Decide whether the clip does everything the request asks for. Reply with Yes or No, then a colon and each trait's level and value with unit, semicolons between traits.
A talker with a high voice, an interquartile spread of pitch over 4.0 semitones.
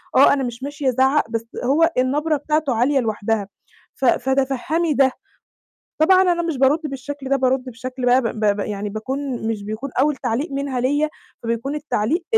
No: very high, 265 Hz; average, 3.4 semitones